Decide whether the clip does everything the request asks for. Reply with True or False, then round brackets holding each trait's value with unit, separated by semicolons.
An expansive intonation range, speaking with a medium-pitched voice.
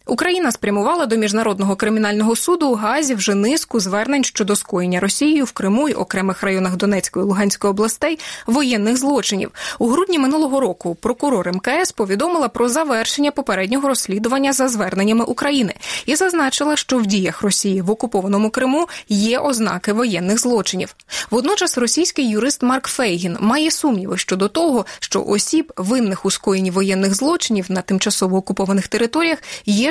False (5.8 semitones; 225 Hz)